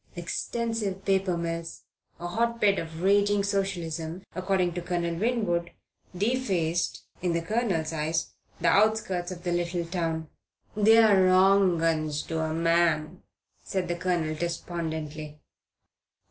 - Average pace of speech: No, slow, 120 wpm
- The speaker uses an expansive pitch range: No, average, 2.9 semitones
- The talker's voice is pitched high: No, medium, 175 Hz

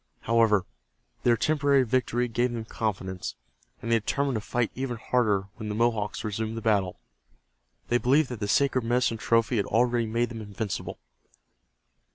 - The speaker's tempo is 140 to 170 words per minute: Yes, average, 160 wpm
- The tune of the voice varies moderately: No, narrow, 2.3 semitones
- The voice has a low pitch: Yes, low, 115 Hz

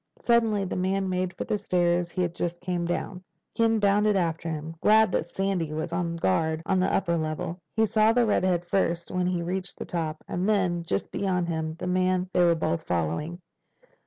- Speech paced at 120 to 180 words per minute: No, average, 200 wpm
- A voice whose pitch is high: No, medium, 180 Hz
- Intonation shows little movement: Yes, narrow, 2.3 semitones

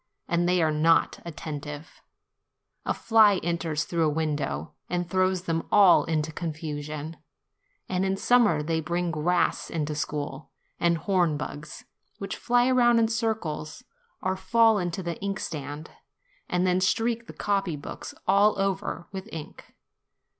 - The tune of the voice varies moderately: Yes, average, 4.2 semitones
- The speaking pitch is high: No, medium, 170 Hz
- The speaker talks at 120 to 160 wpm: Yes, average, 140 wpm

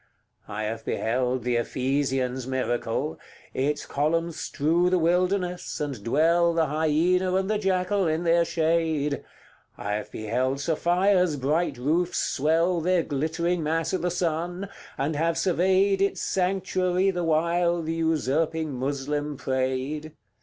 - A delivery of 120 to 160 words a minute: Yes, slow, 135 wpm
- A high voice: No, medium, 160 Hz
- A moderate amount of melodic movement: Yes, average, 4.4 semitones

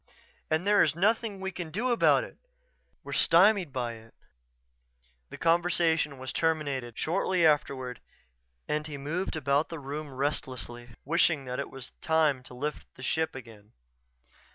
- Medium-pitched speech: Yes, medium, 150 Hz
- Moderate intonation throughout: Yes, average, 4.4 semitones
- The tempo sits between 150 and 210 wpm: No, average, 140 wpm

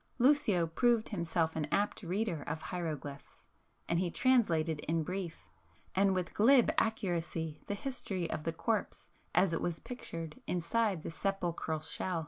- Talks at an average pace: Yes, average, 145 wpm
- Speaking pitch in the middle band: Yes, medium, 175 Hz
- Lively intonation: No, average, 4.4 semitones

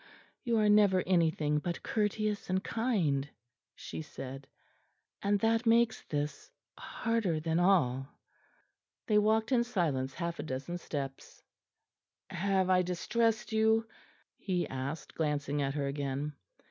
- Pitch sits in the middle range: Yes, medium, 175 Hz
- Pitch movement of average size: No, wide, 6.6 semitones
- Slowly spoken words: Yes, slow, 125 wpm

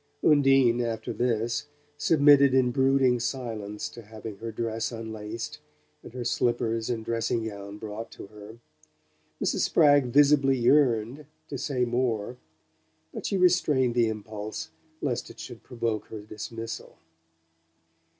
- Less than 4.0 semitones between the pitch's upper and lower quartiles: Yes, average, 3.3 semitones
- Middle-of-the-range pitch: No, low, 120 Hz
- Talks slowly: Yes, slow, 130 wpm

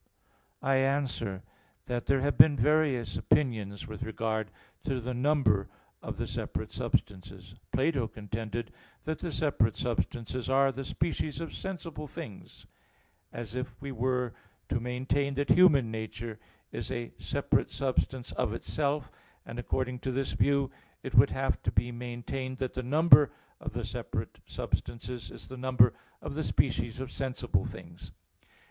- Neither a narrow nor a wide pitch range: Yes, average, 3.2 semitones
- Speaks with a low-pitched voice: Yes, low, 125 Hz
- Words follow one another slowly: No, average, 150 wpm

